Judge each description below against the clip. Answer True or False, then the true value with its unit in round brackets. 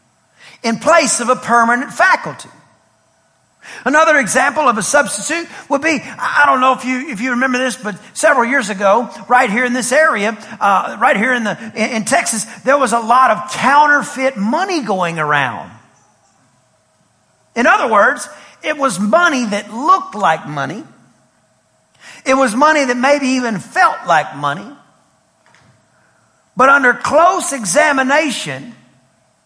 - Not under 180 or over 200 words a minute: False (135 wpm)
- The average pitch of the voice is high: True (255 Hz)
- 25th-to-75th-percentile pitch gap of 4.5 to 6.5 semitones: True (4.9 semitones)